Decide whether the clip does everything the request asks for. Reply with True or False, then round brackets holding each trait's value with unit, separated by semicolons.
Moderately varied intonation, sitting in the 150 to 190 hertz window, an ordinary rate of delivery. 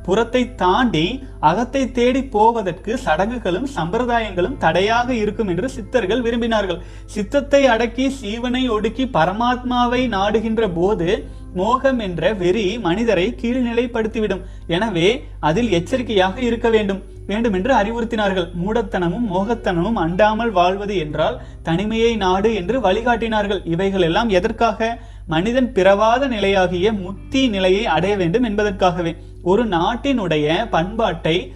False (4.3 semitones; 215 Hz; 105 wpm)